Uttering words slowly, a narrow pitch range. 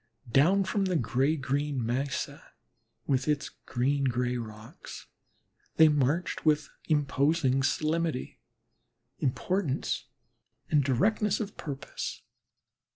No: slow, 95 wpm; average, 3.7 semitones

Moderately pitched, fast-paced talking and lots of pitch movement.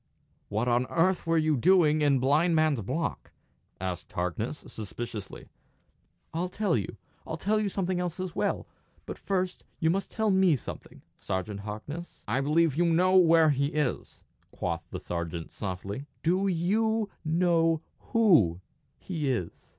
No: medium, 160 Hz; average, 150 wpm; wide, 6.9 semitones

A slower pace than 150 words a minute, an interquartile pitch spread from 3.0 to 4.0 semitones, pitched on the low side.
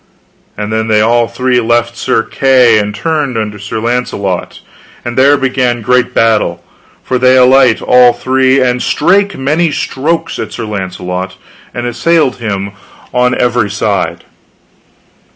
Yes: average, 140 wpm; average, 3.4 semitones; low, 120 Hz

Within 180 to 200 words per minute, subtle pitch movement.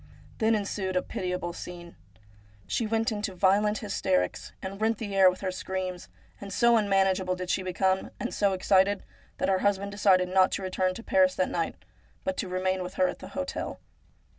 Yes: average, 190 wpm; narrow, 2.0 semitones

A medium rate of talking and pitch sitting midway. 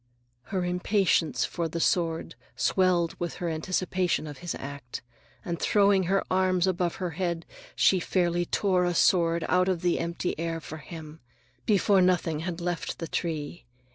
Yes: average, 160 wpm; medium, 175 Hz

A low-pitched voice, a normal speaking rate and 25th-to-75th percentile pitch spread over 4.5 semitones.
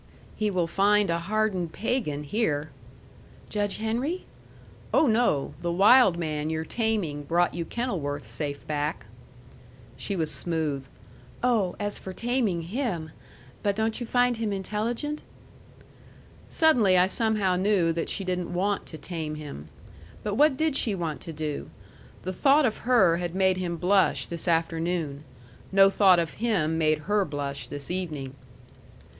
No: medium, 185 Hz; average, 150 wpm; average, 5.2 semitones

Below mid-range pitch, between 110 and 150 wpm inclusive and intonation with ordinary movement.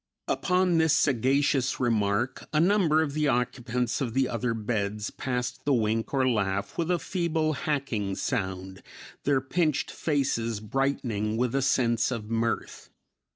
Yes: low, 125 Hz; average, 145 wpm; average, 4.4 semitones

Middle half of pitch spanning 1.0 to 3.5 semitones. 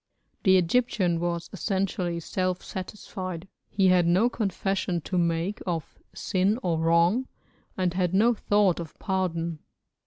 Yes: narrow, 2.4 semitones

